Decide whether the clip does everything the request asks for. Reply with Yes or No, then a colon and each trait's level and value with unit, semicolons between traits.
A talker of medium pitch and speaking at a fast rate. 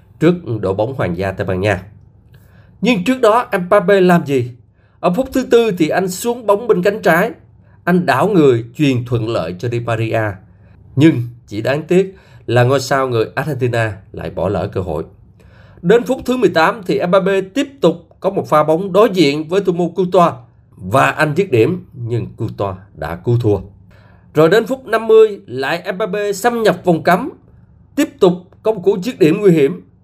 No: medium, 155 Hz; average, 185 wpm